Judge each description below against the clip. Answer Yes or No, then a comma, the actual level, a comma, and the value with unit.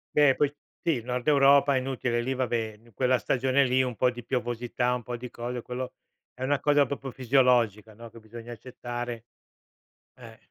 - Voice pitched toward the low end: Yes, low, 125 Hz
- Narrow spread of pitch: Yes, narrow, 1.9 semitones